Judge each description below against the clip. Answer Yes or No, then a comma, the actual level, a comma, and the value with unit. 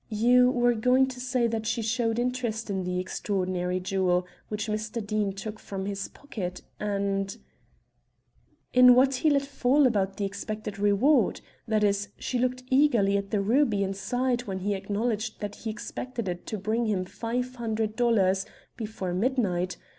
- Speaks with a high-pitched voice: Yes, high, 215 Hz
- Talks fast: No, average, 165 wpm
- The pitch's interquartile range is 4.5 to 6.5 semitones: No, average, 3.8 semitones